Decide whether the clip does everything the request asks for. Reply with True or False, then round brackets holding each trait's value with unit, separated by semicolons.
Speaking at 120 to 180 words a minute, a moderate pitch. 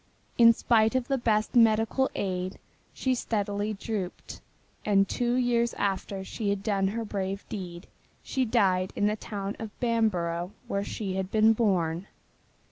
False (150 wpm; 210 Hz)